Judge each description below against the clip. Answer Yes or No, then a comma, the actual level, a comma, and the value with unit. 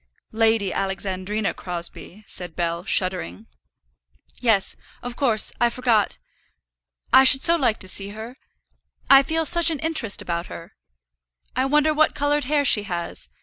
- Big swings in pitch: Yes, wide, 6.6 semitones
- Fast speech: No, average, 145 wpm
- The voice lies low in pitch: No, high, 225 Hz